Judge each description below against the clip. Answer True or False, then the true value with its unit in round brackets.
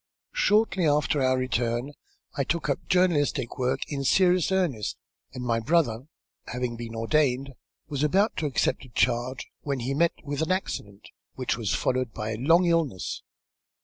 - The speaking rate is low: False (160 wpm)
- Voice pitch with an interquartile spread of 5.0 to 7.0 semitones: True (5.3 semitones)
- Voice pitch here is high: False (135 Hz)